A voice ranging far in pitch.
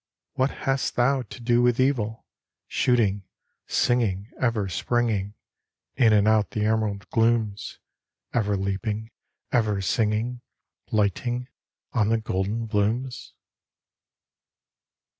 No: average, 2.7 semitones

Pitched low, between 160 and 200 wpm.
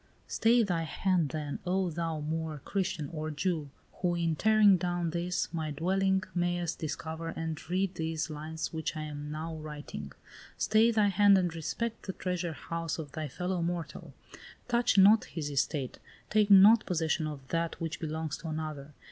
No: medium, 165 Hz; average, 165 wpm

